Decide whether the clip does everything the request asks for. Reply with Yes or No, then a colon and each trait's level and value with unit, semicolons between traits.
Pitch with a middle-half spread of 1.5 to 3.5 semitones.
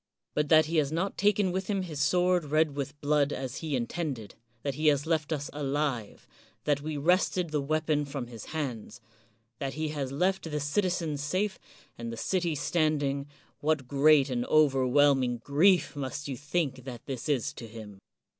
Yes: average, 2.9 semitones